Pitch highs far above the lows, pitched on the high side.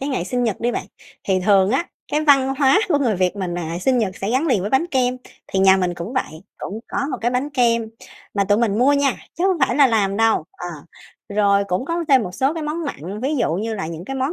Yes: wide, 5.7 semitones; high, 230 Hz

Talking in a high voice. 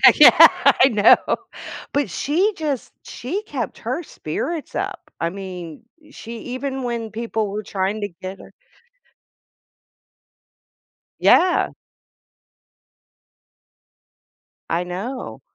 Yes: high, 230 Hz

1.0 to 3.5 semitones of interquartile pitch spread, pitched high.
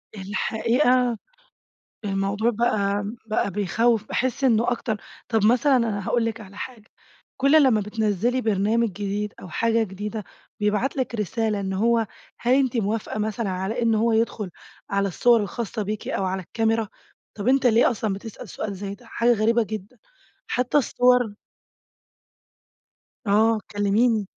Yes: average, 2.7 semitones; high, 220 Hz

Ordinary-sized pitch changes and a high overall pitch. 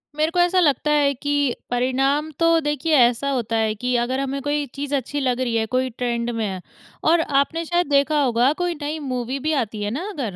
Yes: average, 3.7 semitones; very high, 275 Hz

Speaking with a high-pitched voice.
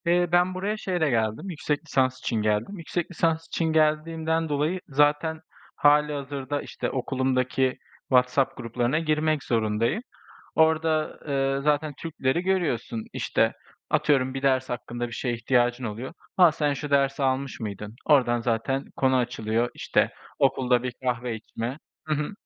No: low, 135 Hz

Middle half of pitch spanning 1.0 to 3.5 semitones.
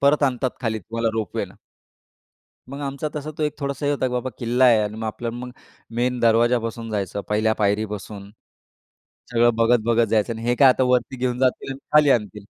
Yes: average, 2.8 semitones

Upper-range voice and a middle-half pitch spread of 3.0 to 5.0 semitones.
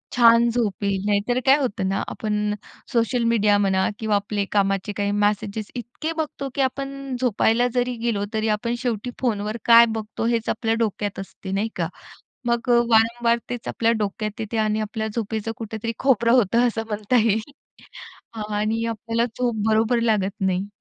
No: high, 225 Hz; narrow, 2.4 semitones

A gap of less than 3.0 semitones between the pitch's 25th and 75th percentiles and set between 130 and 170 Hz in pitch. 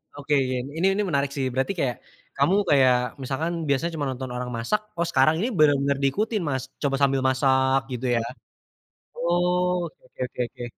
No: average, 4.2 semitones; medium, 140 Hz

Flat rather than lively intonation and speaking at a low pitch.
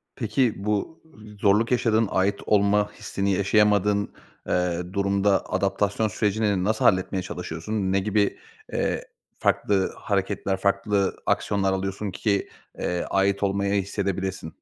Yes: narrow, 1.4 semitones; low, 100 Hz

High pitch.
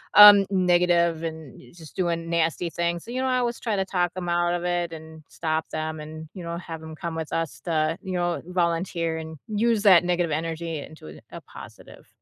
No: medium, 170 Hz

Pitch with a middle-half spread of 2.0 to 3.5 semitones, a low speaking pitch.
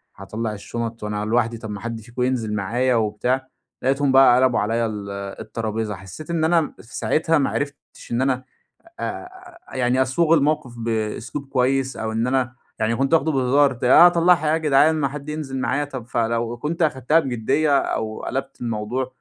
No: average, 4.1 semitones; low, 130 Hz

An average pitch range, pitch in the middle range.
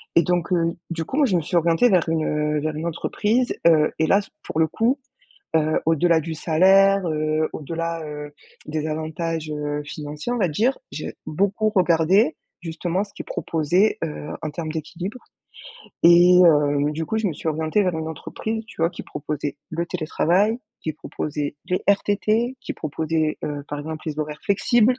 Yes: average, 3.8 semitones; medium, 165 Hz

